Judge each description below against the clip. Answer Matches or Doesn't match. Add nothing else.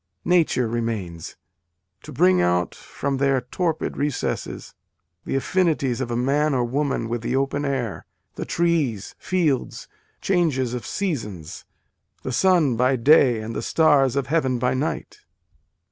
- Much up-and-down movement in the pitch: Doesn't match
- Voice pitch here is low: Matches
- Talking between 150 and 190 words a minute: Doesn't match